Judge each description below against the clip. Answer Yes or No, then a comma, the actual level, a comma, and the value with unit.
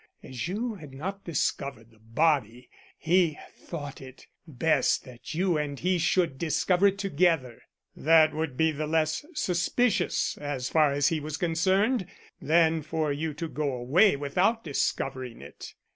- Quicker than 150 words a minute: No, average, 145 wpm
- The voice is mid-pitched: Yes, medium, 155 Hz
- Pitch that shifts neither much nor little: Yes, average, 3.9 semitones